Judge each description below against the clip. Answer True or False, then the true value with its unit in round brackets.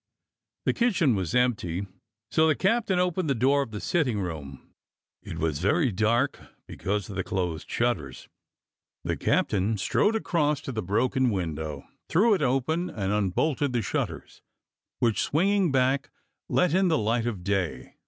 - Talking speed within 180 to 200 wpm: False (160 wpm)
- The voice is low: True (120 Hz)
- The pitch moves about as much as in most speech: False (8.4 semitones)